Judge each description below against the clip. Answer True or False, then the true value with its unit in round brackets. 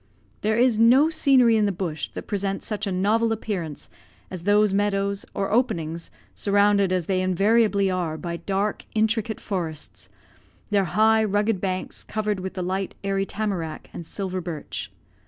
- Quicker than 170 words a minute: False (155 wpm)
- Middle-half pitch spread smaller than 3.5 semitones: True (2.8 semitones)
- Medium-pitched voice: False (200 Hz)